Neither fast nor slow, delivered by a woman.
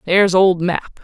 Yes: average, 175 wpm; female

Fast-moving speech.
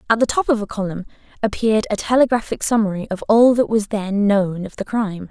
Yes: fast, 215 wpm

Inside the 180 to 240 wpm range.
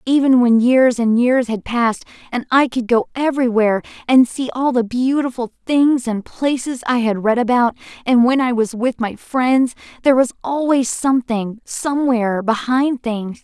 No: average, 170 wpm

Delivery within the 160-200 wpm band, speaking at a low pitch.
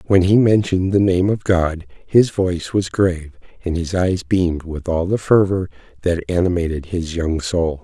Yes: average, 185 wpm; very low, 90 Hz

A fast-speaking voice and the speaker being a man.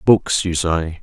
No: average, 175 wpm; male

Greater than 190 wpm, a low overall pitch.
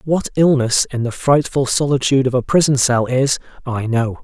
No: average, 185 wpm; low, 130 Hz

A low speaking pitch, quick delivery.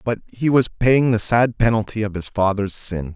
Yes: low, 110 Hz; fast, 210 wpm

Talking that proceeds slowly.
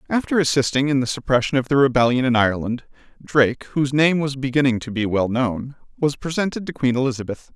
No: average, 190 wpm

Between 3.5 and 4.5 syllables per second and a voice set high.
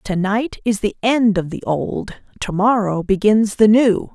Yes: 4.0 syllables/s; high, 210 Hz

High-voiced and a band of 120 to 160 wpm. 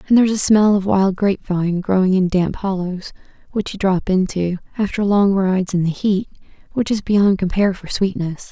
No: high, 195 Hz; average, 195 wpm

